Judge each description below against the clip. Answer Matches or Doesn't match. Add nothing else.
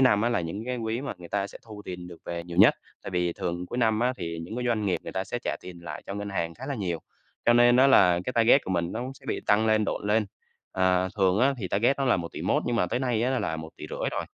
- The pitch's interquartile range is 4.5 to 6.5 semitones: Matches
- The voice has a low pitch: Matches